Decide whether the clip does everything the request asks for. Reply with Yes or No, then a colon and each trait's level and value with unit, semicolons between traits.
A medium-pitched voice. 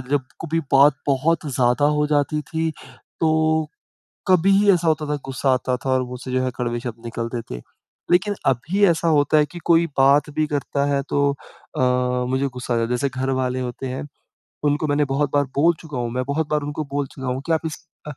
Yes: medium, 145 Hz